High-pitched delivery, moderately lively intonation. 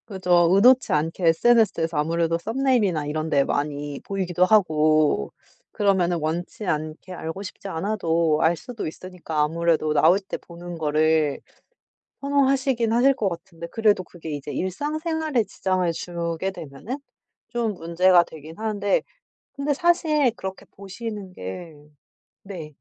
No: medium, 180 Hz; average, 5.0 semitones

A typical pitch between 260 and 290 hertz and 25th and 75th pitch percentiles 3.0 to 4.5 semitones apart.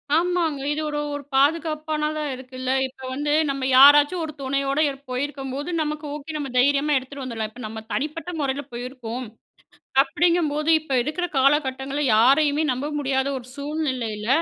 No: very high, 280 Hz; narrow, 2.6 semitones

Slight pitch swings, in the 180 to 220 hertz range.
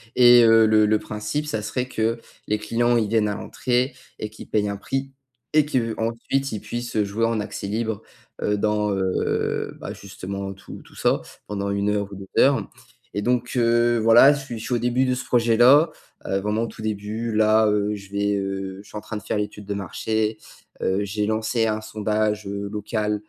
No: narrow, 2.2 semitones; low, 110 Hz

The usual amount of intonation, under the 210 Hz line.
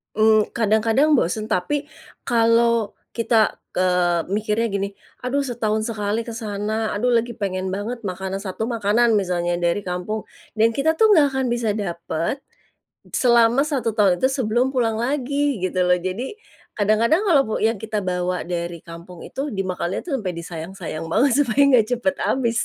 No: average, 4.4 semitones; high, 215 Hz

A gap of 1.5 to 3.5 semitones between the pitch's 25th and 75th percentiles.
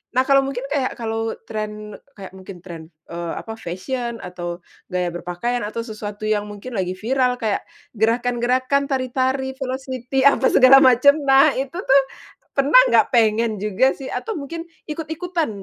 No: average, 4.3 semitones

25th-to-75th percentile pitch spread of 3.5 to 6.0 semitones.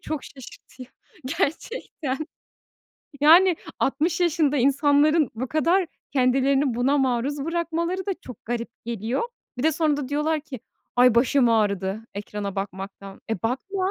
Yes: average, 4.9 semitones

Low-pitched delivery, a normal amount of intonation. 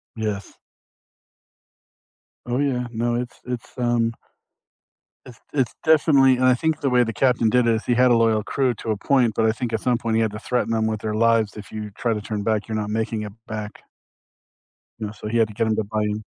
No: low, 115 Hz; narrow, 2.3 semitones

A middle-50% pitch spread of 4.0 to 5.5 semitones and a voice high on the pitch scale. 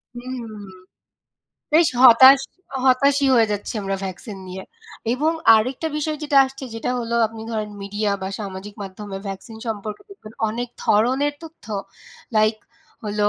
Yes: average, 4.3 semitones; high, 225 Hz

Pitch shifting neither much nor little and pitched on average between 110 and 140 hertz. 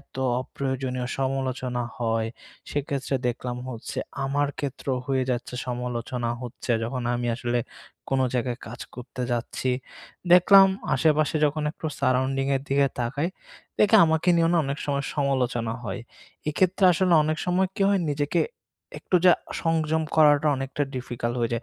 Yes: average, 3.6 semitones; low, 135 Hz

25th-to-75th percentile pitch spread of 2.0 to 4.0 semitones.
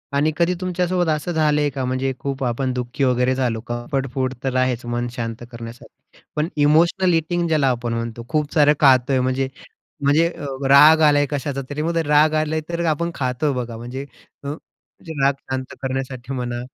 Yes: average, 3.4 semitones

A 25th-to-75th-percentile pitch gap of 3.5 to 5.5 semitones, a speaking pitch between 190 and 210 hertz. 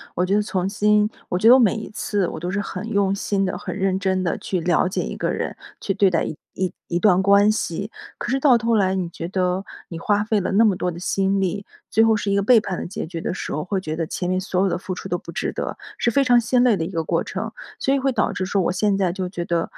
No: average, 2.7 semitones; high, 195 Hz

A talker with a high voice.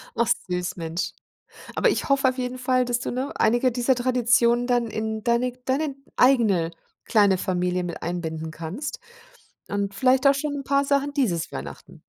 Yes: high, 240 Hz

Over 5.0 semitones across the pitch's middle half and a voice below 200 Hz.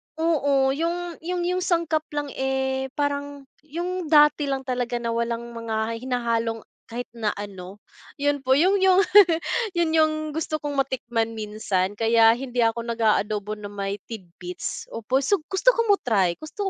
No: wide, 5.6 semitones; very high, 265 Hz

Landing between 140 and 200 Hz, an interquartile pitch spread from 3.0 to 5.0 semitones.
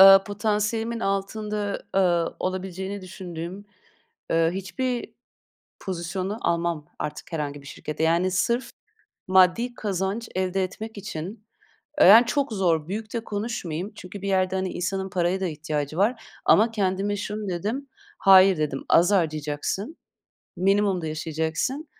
Yes: high, 190 Hz; average, 3.4 semitones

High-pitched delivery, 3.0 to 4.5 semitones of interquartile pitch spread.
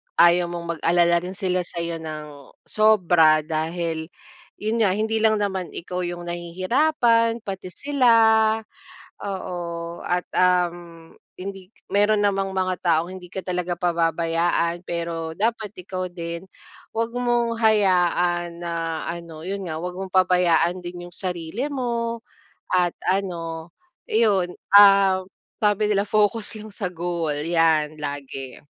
No: medium, 180 Hz; average, 3.3 semitones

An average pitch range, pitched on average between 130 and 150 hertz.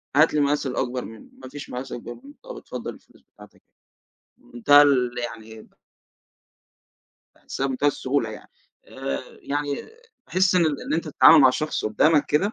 Yes: average, 3.5 semitones; medium, 140 Hz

